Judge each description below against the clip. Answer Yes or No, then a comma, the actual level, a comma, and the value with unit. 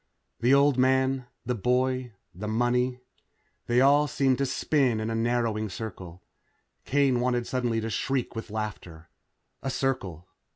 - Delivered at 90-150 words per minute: Yes, average, 140 wpm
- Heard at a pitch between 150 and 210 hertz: No, low, 125 Hz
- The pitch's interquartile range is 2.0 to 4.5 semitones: Yes, average, 3.1 semitones